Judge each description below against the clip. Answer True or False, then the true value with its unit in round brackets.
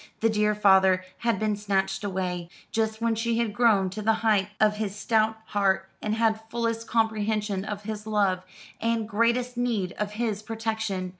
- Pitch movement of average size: False (2.2 semitones)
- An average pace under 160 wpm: False (170 wpm)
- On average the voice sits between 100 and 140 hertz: False (215 Hz)